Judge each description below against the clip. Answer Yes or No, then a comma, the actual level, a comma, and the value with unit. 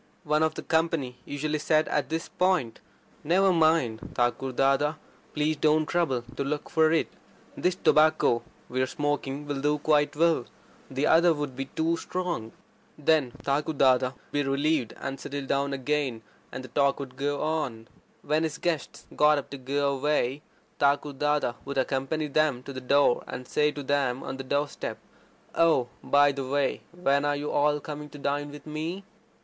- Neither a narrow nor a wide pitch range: No, narrow, 2.3 semitones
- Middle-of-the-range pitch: Yes, medium, 145 Hz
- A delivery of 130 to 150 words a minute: No, average, 175 wpm